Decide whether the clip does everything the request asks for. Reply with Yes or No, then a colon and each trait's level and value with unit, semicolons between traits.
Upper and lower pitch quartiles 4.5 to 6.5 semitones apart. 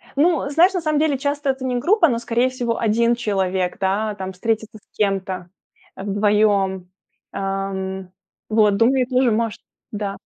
Yes: average, 4.8 semitones